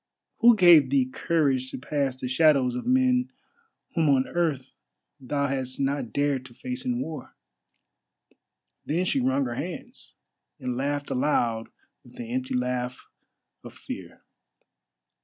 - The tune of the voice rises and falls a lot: No, average, 3.0 semitones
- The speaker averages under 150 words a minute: Yes, average, 140 wpm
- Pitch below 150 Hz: Yes, low, 135 Hz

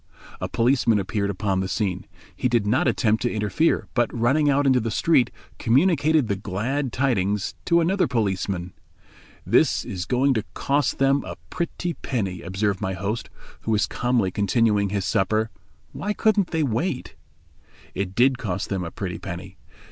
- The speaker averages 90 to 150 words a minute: No, average, 165 wpm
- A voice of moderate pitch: No, low, 110 Hz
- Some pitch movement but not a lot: No, wide, 5.7 semitones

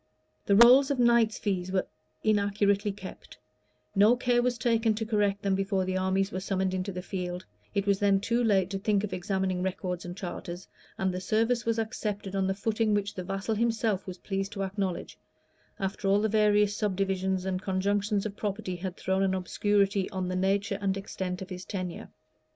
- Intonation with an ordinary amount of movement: No, narrow, 1.9 semitones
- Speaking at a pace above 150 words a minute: Yes, average, 190 wpm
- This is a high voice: Yes, high, 195 Hz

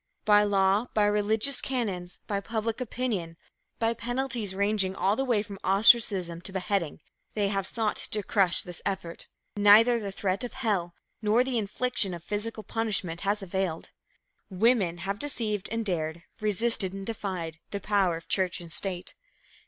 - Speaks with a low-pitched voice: No, high, 205 Hz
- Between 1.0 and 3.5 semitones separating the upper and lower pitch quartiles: Yes, average, 3.2 semitones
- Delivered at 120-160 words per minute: Yes, average, 155 wpm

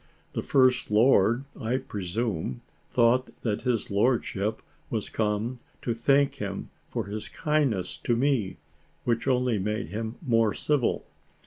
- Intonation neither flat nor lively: Yes, average, 3.5 semitones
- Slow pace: Yes, slow, 130 wpm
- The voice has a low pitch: Yes, low, 115 Hz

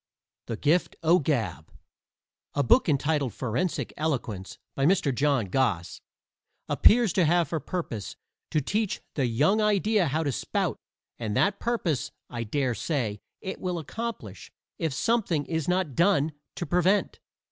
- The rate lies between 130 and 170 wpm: Yes, average, 145 wpm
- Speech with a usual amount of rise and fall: No, wide, 6.1 semitones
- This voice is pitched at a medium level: Yes, medium, 155 Hz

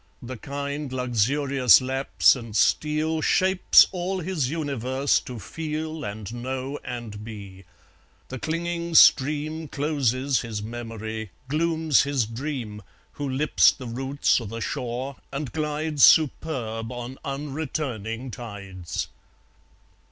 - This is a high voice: No, low, 135 Hz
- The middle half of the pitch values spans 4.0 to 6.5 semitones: Yes, average, 4.6 semitones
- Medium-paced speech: No, slow, 115 wpm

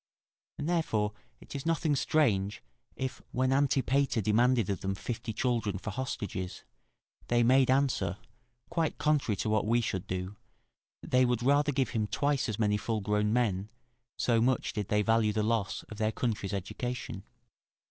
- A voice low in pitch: Yes, low, 115 Hz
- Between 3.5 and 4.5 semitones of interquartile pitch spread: Yes, average, 3.9 semitones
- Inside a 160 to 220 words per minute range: Yes, average, 165 wpm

